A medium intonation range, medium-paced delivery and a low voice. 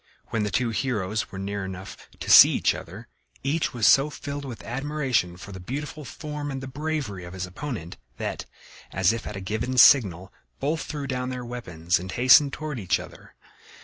No: wide, 6.7 semitones; average, 190 wpm; low, 120 Hz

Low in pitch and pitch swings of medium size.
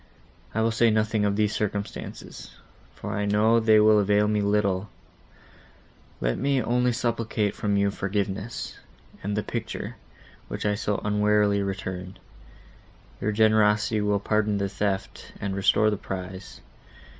No: low, 105 Hz; narrow, 1.3 semitones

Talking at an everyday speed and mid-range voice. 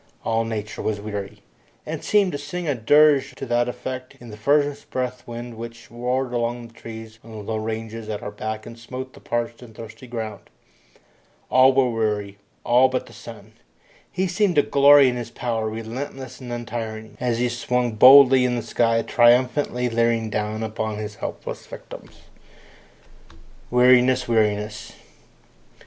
No: average, 160 wpm; low, 120 Hz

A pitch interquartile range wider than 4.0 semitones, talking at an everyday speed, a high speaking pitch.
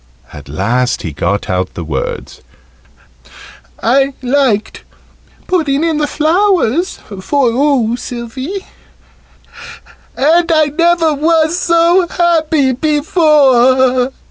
No: average, 5.3 semitones; slow, 95 wpm; very high, 285 Hz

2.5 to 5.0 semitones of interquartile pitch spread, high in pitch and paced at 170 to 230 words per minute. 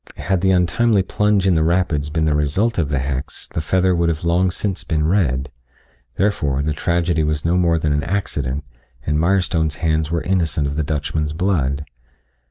No: average, 3.5 semitones; very low, 80 Hz; average, 185 wpm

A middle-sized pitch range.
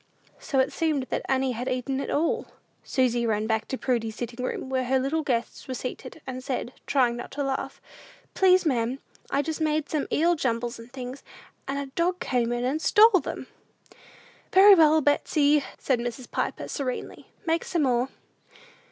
Yes: average, 3.7 semitones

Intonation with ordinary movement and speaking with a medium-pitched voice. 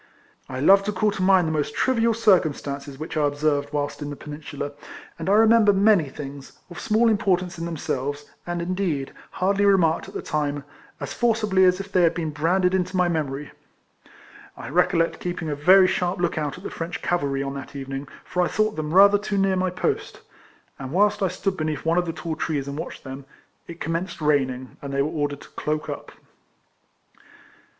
Yes: average, 4.6 semitones; medium, 165 Hz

